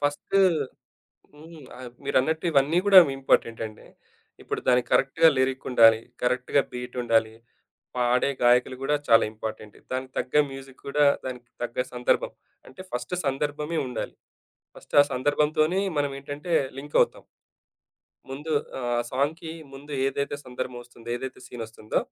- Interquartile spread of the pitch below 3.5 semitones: Yes, average, 3.0 semitones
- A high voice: No, low, 130 Hz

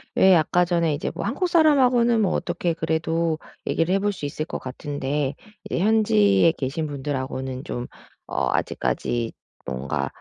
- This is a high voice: No, medium, 160 Hz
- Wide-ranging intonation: Yes, wide, 5.9 semitones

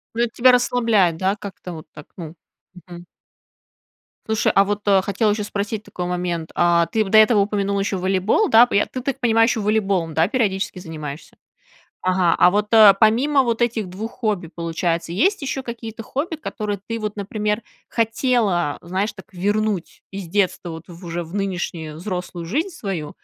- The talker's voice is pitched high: Yes, high, 200 Hz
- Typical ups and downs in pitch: Yes, average, 4.1 semitones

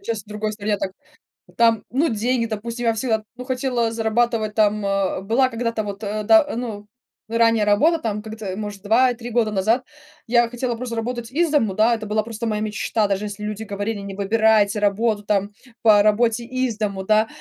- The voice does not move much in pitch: Yes, narrow, 2.2 semitones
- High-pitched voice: Yes, high, 220 Hz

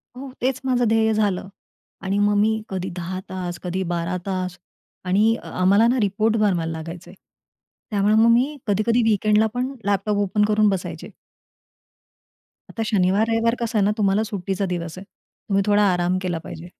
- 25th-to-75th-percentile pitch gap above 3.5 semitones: No, average, 3.1 semitones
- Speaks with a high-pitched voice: Yes, high, 205 Hz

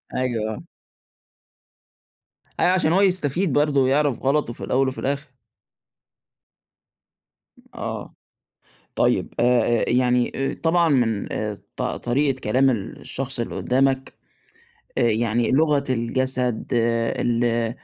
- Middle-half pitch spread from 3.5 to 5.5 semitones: No, average, 3.0 semitones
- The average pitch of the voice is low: Yes, low, 130 Hz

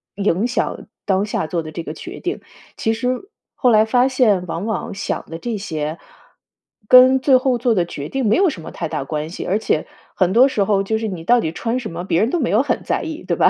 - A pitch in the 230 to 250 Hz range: No, high, 215 Hz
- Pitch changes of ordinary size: No, wide, 6.4 semitones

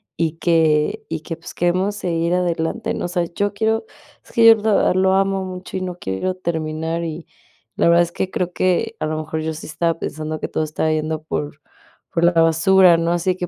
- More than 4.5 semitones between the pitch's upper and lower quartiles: No, narrow, 2.6 semitones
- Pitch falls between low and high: Yes, medium, 170 Hz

